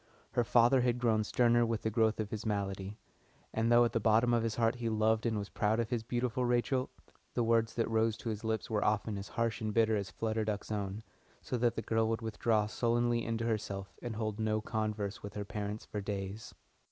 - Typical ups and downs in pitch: No, narrow, 1.7 semitones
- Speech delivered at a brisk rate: Yes, fast, 225 wpm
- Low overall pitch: Yes, low, 110 Hz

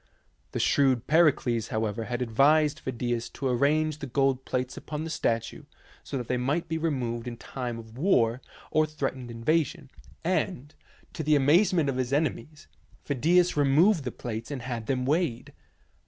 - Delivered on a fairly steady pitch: No, average, 4.2 semitones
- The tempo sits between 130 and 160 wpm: No, average, 170 wpm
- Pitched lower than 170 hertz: Yes, low, 135 Hz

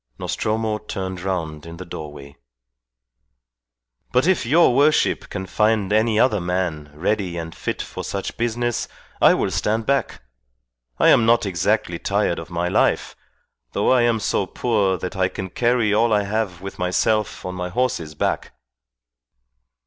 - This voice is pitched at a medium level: No, low, 100 Hz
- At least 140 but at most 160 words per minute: Yes, average, 155 wpm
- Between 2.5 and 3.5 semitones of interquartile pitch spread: No, average, 4.1 semitones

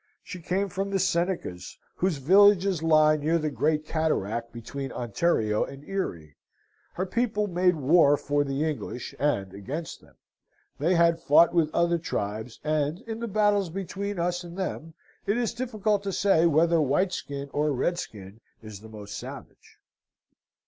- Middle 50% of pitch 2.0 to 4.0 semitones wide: No, average, 5.2 semitones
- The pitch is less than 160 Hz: No, medium, 165 Hz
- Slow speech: No, average, 150 wpm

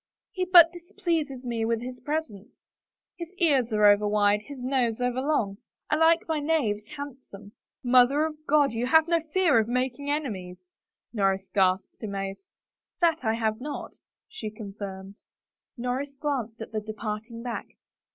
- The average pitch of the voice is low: No, high, 245 Hz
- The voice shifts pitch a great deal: Yes, wide, 5.9 semitones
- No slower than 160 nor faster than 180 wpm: Yes, average, 170 wpm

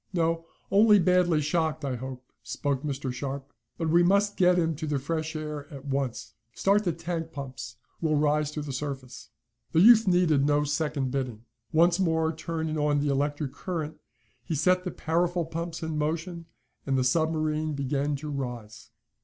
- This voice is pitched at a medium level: Yes, medium, 155 Hz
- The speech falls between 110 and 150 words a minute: No, average, 170 wpm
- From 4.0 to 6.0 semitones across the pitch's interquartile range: No, average, 3.2 semitones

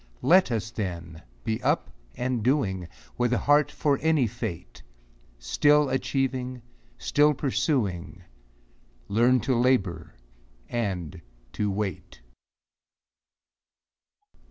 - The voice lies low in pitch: Yes, low, 120 Hz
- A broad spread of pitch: Yes, wide, 6.3 semitones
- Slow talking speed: Yes, slow, 95 wpm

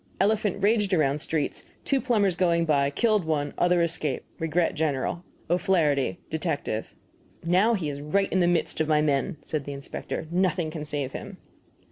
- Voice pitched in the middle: Yes, medium, 165 Hz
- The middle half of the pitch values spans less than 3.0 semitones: No, average, 4.0 semitones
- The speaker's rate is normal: Yes, average, 165 wpm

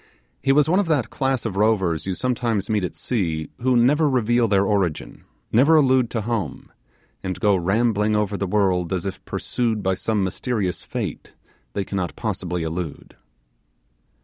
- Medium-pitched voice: No, low, 105 Hz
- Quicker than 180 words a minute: No, average, 165 wpm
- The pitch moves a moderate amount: Yes, average, 4.4 semitones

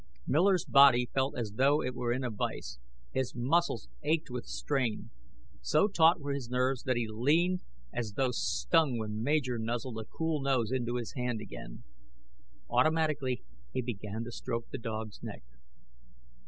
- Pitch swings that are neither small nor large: Yes, average, 3.6 semitones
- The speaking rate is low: No, average, 160 wpm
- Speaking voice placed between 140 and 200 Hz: No, low, 125 Hz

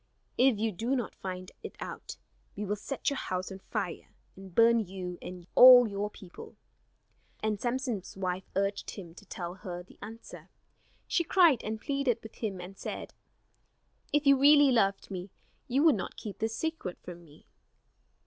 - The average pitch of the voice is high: Yes, high, 210 Hz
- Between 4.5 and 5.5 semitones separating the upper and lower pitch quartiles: Yes, average, 5.2 semitones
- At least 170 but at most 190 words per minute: Yes, average, 175 wpm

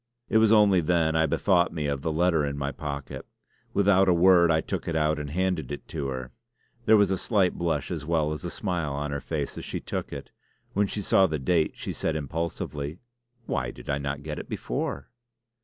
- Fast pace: Yes, fast, 220 wpm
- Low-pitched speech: Yes, very low, 80 Hz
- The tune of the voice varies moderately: Yes, average, 3.9 semitones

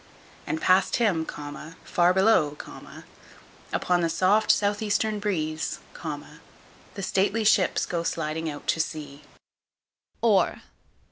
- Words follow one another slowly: Yes, slow, 110 wpm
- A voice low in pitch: No, medium, 185 Hz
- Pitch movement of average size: Yes, average, 4.3 semitones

